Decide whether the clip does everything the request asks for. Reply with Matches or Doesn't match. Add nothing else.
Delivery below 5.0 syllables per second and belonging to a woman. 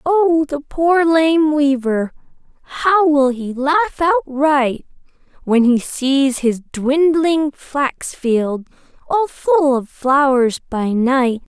Matches